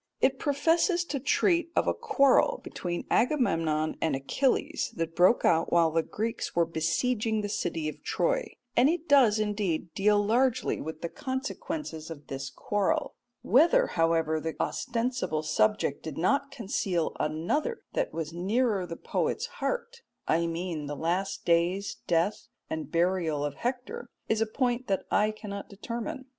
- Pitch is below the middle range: No, high, 205 Hz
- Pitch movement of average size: No, wide, 7.9 semitones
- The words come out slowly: No, average, 150 wpm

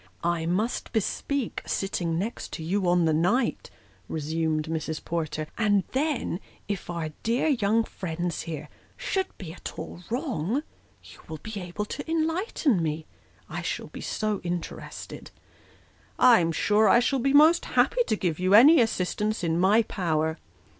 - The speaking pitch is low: No, high, 190 Hz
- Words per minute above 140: Yes, average, 160 wpm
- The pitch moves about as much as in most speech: No, wide, 6.1 semitones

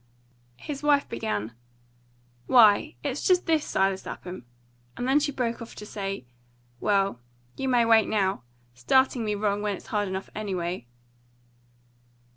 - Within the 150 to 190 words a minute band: No, average, 140 wpm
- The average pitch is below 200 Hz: No, high, 210 Hz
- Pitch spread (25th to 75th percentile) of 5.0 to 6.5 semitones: Yes, average, 5.3 semitones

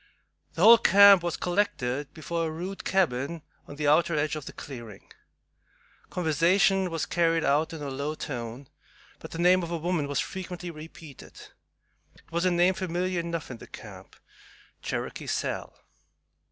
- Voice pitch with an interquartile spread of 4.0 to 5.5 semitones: No, average, 3.4 semitones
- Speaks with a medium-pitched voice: Yes, medium, 165 Hz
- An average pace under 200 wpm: Yes, average, 160 wpm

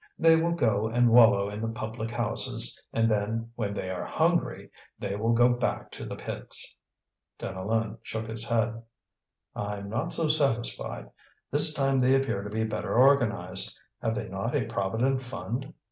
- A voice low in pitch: Yes, low, 115 Hz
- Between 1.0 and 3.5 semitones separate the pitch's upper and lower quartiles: Yes, average, 2.8 semitones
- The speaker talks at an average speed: Yes, average, 165 wpm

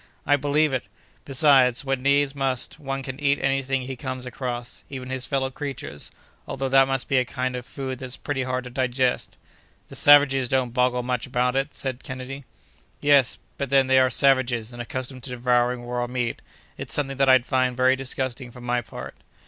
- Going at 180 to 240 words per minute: Yes, average, 195 wpm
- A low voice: Yes, low, 130 Hz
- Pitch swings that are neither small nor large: No, narrow, 1.5 semitones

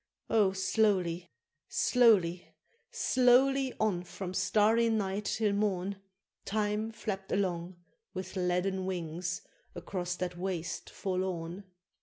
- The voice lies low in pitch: No, high, 190 Hz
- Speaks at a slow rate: Yes, slow, 100 wpm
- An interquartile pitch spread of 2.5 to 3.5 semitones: Yes, average, 2.9 semitones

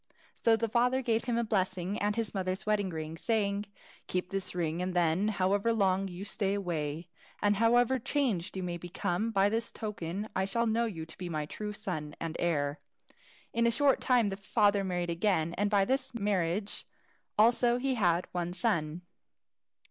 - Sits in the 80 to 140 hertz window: No, high, 200 Hz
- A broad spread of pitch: No, average, 4.2 semitones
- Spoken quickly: No, average, 180 wpm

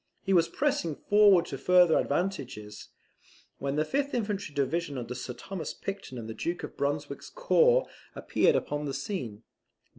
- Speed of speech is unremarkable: Yes, average, 155 wpm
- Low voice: No, medium, 165 Hz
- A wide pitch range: Yes, wide, 6.3 semitones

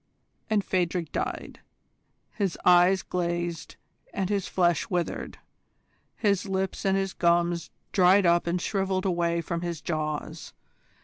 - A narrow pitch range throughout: Yes, narrow, 2.0 semitones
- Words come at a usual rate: No, slow, 125 wpm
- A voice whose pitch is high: No, medium, 175 Hz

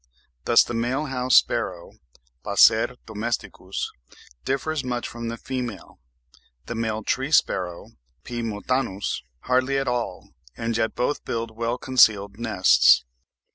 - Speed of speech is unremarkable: No, slow, 125 wpm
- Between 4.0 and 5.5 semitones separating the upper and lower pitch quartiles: No, narrow, 2.4 semitones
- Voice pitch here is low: Yes, low, 115 Hz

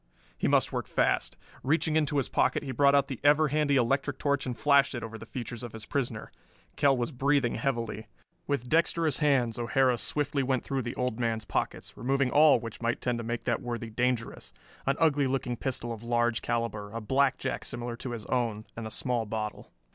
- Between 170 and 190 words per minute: No, average, 200 wpm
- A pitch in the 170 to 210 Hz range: No, low, 125 Hz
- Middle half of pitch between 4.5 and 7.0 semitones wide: No, average, 3.2 semitones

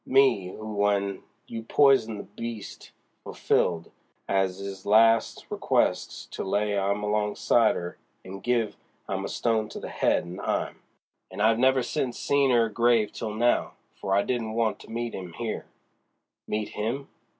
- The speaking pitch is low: Yes, low, 110 Hz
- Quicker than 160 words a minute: No, average, 155 wpm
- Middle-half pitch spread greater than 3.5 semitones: No, average, 2.8 semitones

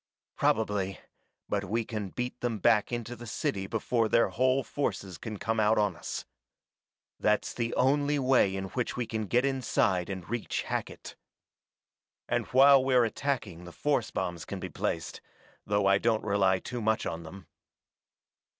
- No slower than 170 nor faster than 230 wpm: No, average, 160 wpm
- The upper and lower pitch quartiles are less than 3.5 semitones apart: No, average, 4.0 semitones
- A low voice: Yes, low, 110 Hz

